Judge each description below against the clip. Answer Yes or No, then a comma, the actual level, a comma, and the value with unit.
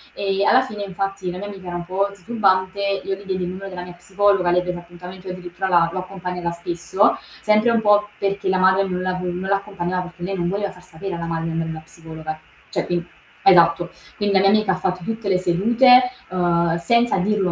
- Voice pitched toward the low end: No, medium, 185 Hz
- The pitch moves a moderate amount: No, narrow, 2.2 semitones